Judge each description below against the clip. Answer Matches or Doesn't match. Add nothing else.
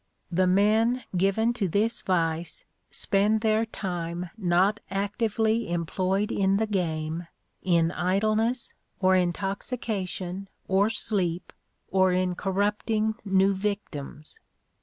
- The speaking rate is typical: Doesn't match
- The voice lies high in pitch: Matches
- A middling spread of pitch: Matches